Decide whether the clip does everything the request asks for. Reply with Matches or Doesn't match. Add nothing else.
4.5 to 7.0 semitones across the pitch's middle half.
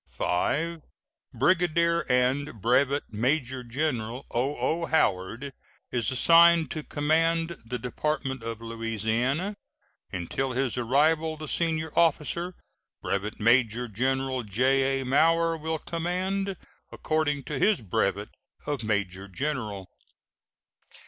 Matches